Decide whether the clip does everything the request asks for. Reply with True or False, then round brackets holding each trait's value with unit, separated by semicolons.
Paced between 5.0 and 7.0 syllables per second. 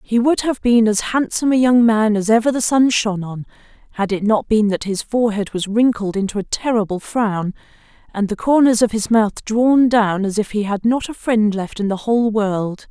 True (5.1 syllables/s)